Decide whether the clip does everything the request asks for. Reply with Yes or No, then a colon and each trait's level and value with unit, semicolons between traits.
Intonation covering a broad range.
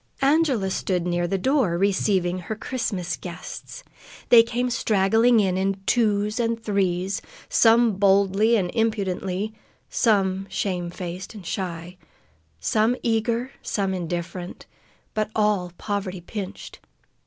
No: average, 3.5 semitones